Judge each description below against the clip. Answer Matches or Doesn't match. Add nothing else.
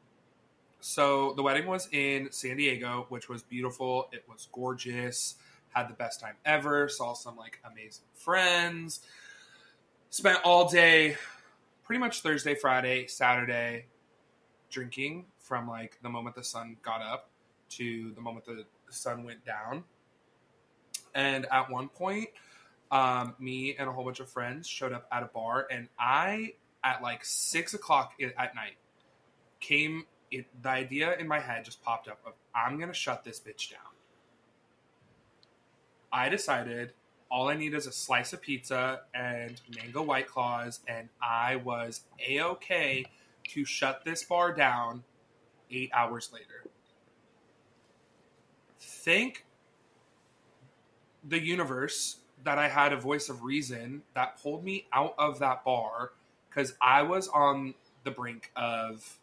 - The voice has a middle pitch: Doesn't match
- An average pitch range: Matches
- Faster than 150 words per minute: Doesn't match